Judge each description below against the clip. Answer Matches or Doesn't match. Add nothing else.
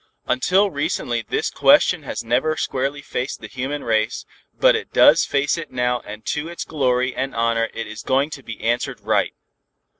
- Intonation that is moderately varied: Matches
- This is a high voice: Doesn't match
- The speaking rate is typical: Matches